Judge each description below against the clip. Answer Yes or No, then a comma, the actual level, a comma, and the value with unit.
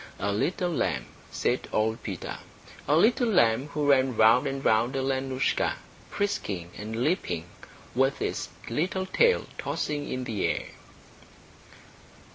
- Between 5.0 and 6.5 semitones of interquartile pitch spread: Yes, average, 5.3 semitones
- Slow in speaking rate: Yes, slow, 125 wpm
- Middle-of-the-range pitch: No, low, 130 Hz